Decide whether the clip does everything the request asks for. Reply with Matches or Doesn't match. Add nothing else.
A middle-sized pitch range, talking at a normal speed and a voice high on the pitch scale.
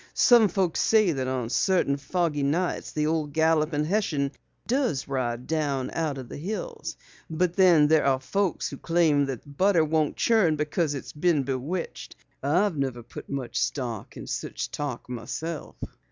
Doesn't match